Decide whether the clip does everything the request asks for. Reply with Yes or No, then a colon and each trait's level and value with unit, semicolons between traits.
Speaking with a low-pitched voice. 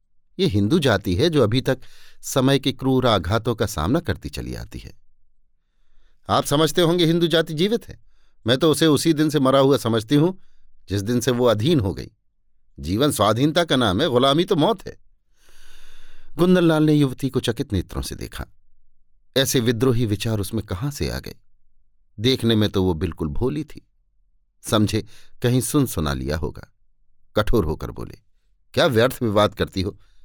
Yes: low, 120 Hz